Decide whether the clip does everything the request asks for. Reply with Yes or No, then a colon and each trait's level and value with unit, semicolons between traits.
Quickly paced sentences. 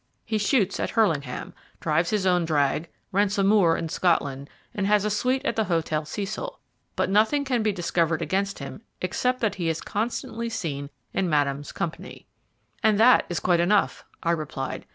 No: average, 175 wpm